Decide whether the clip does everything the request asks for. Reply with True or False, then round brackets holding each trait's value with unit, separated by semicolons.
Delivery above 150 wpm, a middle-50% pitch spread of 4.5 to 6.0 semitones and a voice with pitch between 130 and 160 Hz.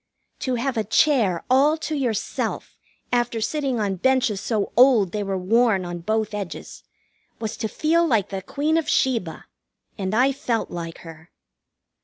False (160 wpm; 5.2 semitones; 225 Hz)